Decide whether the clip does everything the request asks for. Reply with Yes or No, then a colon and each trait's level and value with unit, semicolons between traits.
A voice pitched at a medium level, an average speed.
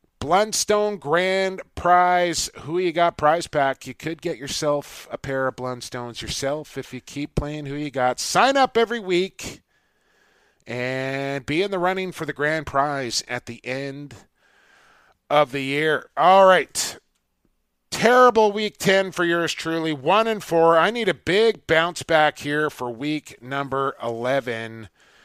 Yes: medium, 150 Hz; average, 155 wpm